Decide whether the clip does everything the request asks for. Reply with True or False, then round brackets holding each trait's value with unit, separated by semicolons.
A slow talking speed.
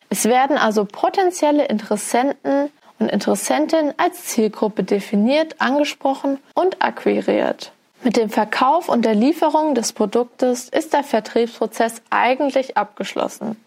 True (115 wpm)